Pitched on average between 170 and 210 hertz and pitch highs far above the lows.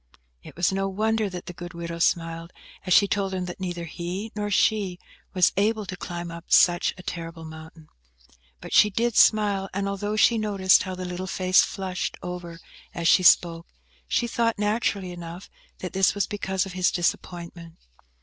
No: medium, 185 Hz; narrow, 2.6 semitones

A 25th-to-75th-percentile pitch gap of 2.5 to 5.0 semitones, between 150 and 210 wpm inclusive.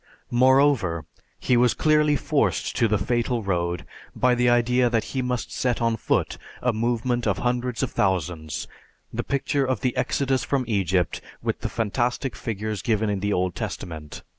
Yes: average, 4.0 semitones; average, 165 wpm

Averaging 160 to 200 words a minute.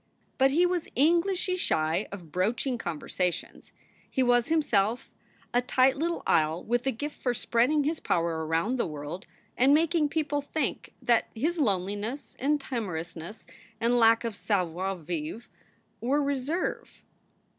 No: average, 140 wpm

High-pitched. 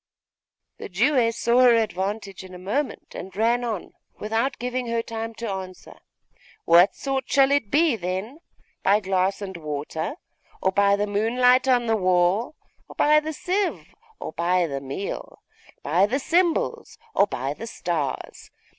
Yes: high, 215 Hz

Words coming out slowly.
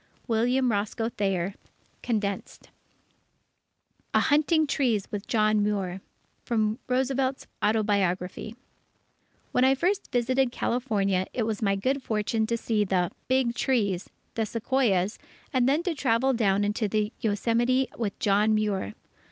Yes: slow, 125 wpm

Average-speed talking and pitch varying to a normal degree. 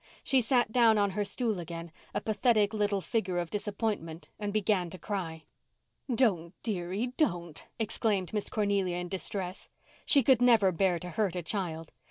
Yes: average, 155 wpm; average, 3.8 semitones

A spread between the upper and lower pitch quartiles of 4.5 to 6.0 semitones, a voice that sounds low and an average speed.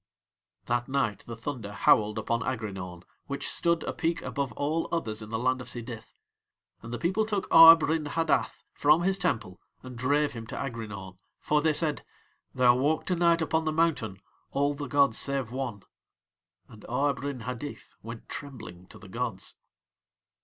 Yes: average, 5.1 semitones; low, 130 Hz; average, 170 wpm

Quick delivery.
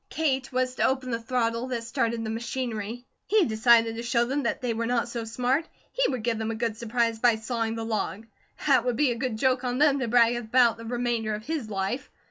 Yes: fast, 230 wpm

